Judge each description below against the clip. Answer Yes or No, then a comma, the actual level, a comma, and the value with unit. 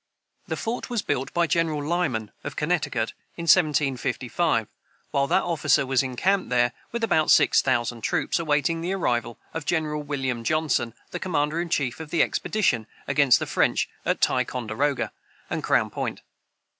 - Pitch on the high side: No, medium, 145 Hz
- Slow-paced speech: No, average, 155 wpm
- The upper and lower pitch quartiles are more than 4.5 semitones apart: Yes, average, 5.0 semitones